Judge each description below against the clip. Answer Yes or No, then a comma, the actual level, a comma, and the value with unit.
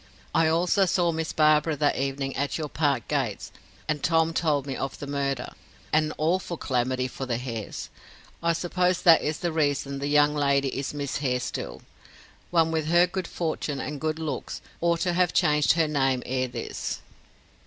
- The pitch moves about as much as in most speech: Yes, average, 3.1 semitones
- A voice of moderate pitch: Yes, medium, 150 Hz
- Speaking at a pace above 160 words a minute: Yes, average, 180 wpm